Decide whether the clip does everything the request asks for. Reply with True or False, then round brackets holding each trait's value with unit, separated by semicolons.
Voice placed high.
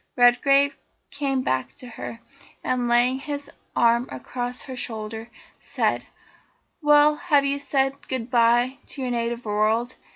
True (250 Hz)